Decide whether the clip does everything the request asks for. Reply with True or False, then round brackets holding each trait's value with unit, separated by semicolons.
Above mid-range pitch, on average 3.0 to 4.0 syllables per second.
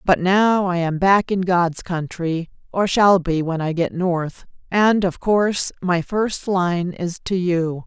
False (180 Hz; 3.6 syllables/s)